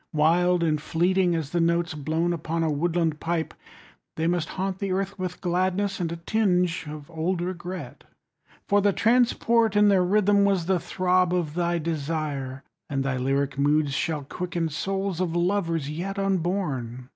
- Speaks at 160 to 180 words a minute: Yes, average, 170 wpm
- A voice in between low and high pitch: Yes, medium, 175 Hz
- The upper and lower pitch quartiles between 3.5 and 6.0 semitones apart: No, average, 3.1 semitones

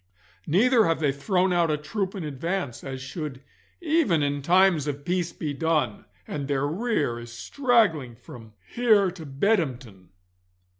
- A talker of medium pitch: Yes, medium, 155 Hz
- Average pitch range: No, wide, 5.7 semitones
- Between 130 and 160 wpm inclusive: Yes, average, 150 wpm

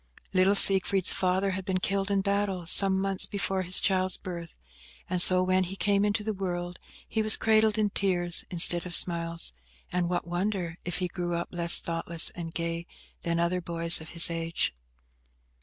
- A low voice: No, medium, 180 Hz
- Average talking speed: Yes, average, 180 wpm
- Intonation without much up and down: Yes, narrow, 2.3 semitones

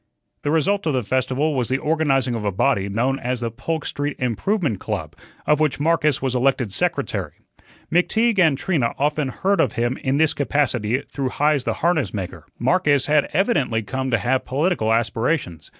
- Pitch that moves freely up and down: No, average, 4.4 semitones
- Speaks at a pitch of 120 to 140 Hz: Yes, low, 135 Hz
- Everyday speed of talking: Yes, average, 180 wpm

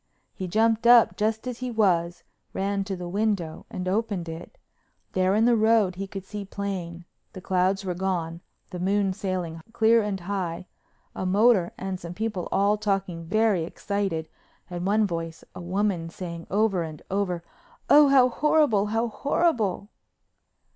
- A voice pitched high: Yes, high, 195 Hz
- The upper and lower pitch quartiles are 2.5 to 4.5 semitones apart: Yes, average, 3.5 semitones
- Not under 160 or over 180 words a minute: No, average, 150 wpm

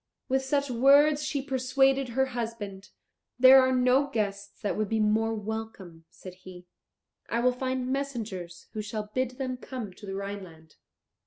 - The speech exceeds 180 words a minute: No, average, 160 wpm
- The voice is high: Yes, high, 235 Hz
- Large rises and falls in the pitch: No, average, 4.6 semitones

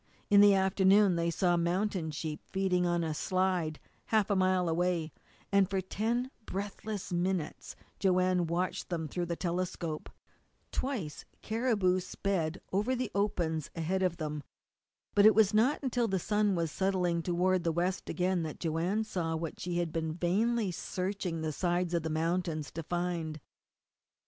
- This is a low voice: No, medium, 180 Hz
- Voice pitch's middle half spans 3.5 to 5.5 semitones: No, average, 2.8 semitones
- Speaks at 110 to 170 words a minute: Yes, average, 160 wpm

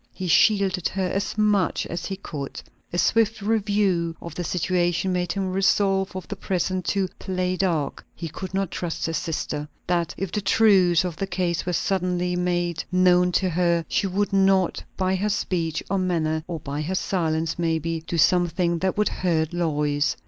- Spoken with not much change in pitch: Yes, narrow, 2.3 semitones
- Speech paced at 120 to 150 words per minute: No, average, 180 wpm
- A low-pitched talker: No, medium, 180 Hz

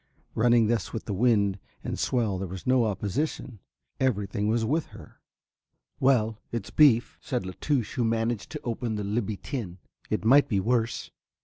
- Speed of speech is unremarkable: Yes, average, 175 wpm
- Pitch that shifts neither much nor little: Yes, average, 3.2 semitones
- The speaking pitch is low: Yes, low, 115 Hz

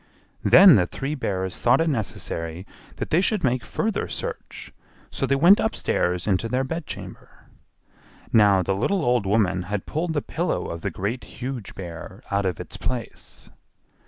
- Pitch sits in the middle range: No, low, 115 Hz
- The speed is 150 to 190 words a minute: Yes, average, 160 wpm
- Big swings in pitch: Yes, wide, 7.8 semitones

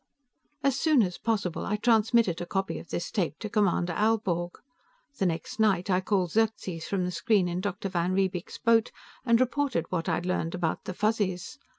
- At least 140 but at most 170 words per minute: No, average, 185 wpm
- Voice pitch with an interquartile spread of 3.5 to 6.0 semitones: Yes, average, 3.9 semitones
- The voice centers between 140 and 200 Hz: Yes, high, 190 Hz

